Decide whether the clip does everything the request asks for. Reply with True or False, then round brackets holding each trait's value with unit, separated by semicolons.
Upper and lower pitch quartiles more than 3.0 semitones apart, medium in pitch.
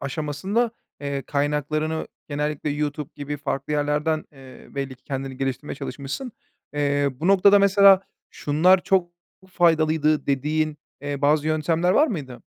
False (2.7 semitones; 150 Hz)